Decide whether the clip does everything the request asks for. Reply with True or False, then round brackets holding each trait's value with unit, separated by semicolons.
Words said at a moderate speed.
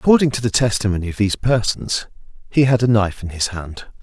False (210 wpm)